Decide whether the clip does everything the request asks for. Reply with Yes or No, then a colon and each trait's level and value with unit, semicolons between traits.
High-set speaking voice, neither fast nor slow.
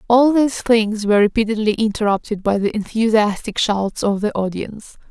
Yes: high, 215 Hz; average, 155 wpm